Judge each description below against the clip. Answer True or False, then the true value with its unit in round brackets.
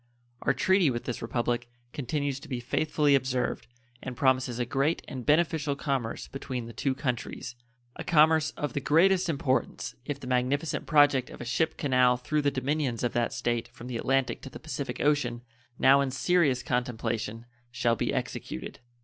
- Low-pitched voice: True (130 Hz)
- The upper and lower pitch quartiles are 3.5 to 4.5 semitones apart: False (3.1 semitones)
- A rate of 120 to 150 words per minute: False (175 wpm)